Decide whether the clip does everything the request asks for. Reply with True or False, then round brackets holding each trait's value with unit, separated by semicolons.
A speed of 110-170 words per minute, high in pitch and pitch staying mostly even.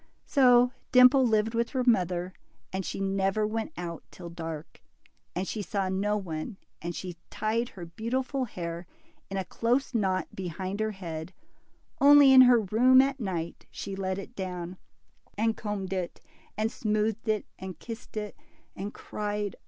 False (160 wpm; 205 Hz; 3.8 semitones)